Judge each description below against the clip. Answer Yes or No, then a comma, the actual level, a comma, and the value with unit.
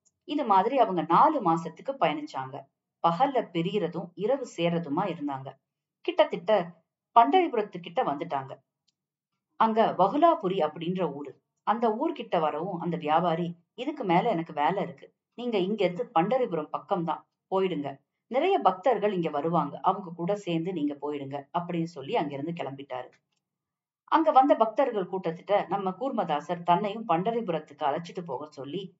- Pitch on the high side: No, medium, 170 Hz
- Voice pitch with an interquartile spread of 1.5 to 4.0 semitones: No, average, 4.8 semitones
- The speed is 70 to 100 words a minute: No, average, 120 wpm